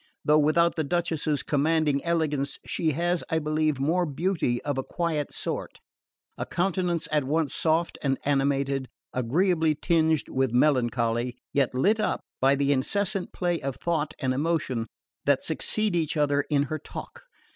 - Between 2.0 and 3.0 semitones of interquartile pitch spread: No, average, 3.4 semitones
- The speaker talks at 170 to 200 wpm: No, average, 155 wpm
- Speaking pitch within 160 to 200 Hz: No, medium, 150 Hz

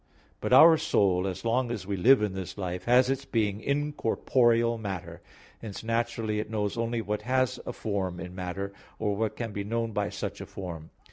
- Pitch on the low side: Yes, low, 110 Hz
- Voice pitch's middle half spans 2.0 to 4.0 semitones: Yes, average, 3.3 semitones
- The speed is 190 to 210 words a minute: Yes, average, 200 wpm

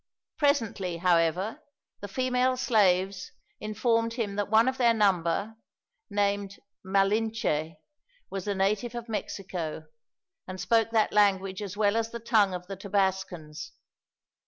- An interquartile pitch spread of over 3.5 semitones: No, average, 3.1 semitones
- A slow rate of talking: Yes, slow, 130 wpm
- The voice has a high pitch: Yes, high, 205 Hz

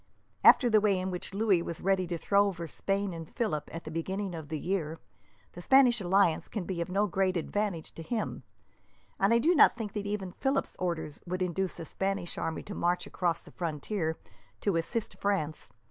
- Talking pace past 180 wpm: Yes, average, 200 wpm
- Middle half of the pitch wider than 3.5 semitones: No, average, 3.2 semitones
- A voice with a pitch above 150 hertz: Yes, medium, 185 Hz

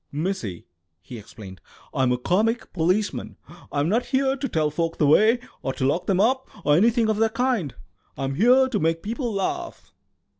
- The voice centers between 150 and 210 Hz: Yes, high, 190 Hz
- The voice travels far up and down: Yes, wide, 8.2 semitones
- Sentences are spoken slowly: No, average, 180 wpm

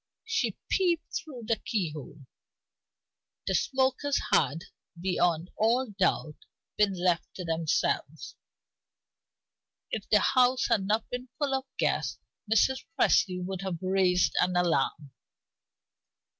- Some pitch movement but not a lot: No, wide, 6.3 semitones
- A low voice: No, high, 190 Hz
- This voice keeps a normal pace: No, slow, 115 wpm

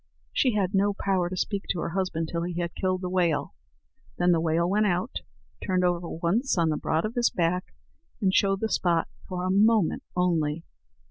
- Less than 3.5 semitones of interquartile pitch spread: Yes, narrow, 2.5 semitones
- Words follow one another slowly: No, average, 200 wpm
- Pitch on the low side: No, medium, 180 Hz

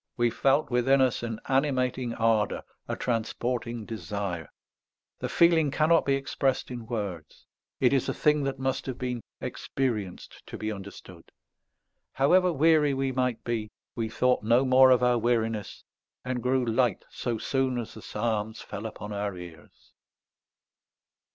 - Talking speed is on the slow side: No, average, 150 wpm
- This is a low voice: Yes, low, 120 Hz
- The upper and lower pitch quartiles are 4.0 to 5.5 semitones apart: No, average, 3.2 semitones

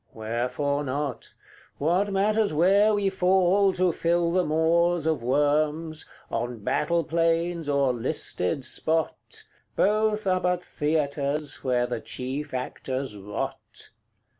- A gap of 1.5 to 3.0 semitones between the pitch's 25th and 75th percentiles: No, average, 4.6 semitones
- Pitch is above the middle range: No, medium, 155 Hz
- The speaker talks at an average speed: No, slow, 115 wpm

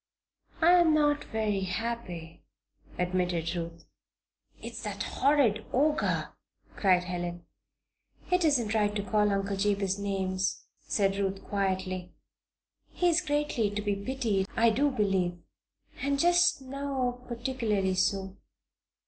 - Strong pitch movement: Yes, wide, 5.7 semitones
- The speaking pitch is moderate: No, high, 205 Hz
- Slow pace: Yes, slow, 120 wpm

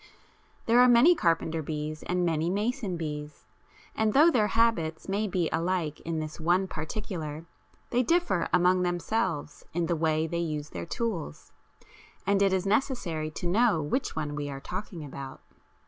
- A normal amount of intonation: Yes, average, 5.0 semitones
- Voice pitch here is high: No, medium, 175 Hz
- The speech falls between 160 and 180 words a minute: Yes, average, 165 wpm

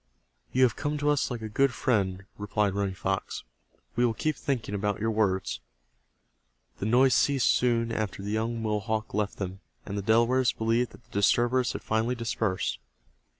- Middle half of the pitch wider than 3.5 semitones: No, average, 3.1 semitones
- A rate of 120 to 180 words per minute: Yes, average, 175 wpm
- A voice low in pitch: Yes, low, 110 Hz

